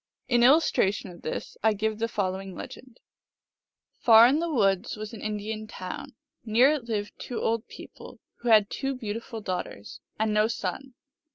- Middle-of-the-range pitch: No, high, 220 Hz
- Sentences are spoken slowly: No, average, 165 wpm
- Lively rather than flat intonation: No, average, 2.9 semitones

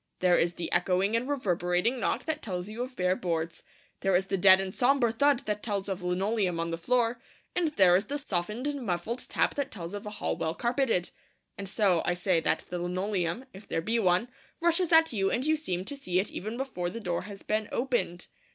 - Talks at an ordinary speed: No, fast, 225 wpm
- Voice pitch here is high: Yes, high, 200 Hz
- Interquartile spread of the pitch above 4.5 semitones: Yes, average, 5.3 semitones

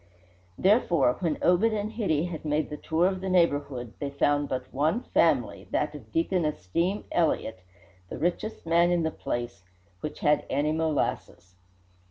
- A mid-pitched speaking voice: Yes, medium, 160 Hz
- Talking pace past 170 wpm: No, average, 160 wpm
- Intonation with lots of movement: No, average, 4.0 semitones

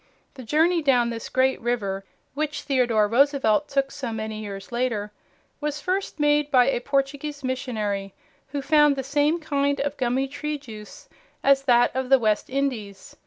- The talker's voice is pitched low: No, very high, 265 Hz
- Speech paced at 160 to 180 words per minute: Yes, average, 165 wpm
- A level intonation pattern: No, average, 4.0 semitones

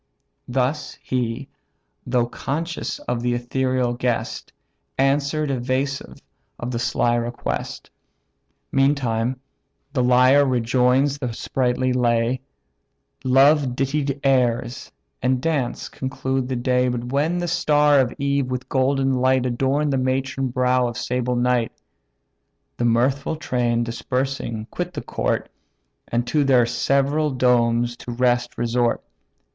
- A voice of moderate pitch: No, low, 130 Hz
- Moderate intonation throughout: No, narrow, 2.0 semitones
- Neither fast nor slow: No, slow, 120 wpm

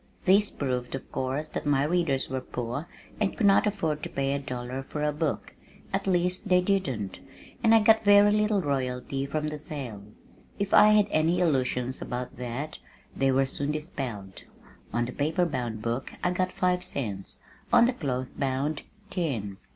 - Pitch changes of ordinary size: No, wide, 6.0 semitones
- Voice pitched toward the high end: No, medium, 145 Hz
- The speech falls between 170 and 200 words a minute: Yes, average, 175 wpm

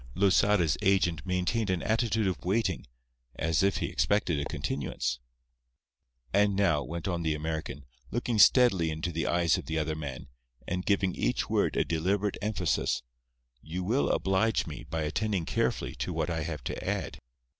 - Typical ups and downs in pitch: Yes, average, 4.1 semitones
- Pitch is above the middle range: No, very low, 90 Hz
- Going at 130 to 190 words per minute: Yes, average, 165 wpm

